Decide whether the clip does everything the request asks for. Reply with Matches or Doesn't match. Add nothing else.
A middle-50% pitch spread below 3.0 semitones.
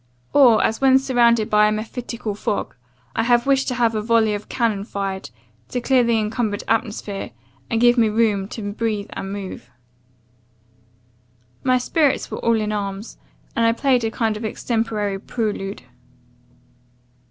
Matches